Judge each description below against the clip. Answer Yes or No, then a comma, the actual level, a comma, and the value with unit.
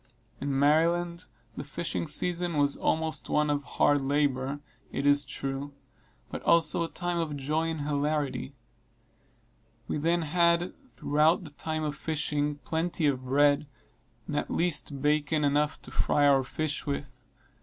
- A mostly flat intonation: Yes, narrow, 2.2 semitones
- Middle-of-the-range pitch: Yes, medium, 150 Hz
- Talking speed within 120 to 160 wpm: Yes, average, 145 wpm